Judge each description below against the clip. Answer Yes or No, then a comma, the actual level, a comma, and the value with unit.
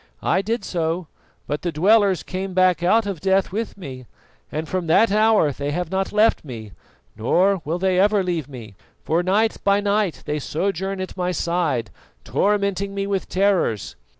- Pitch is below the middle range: No, medium, 185 Hz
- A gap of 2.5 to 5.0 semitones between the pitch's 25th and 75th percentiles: Yes, average, 3.8 semitones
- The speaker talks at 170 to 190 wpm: Yes, average, 175 wpm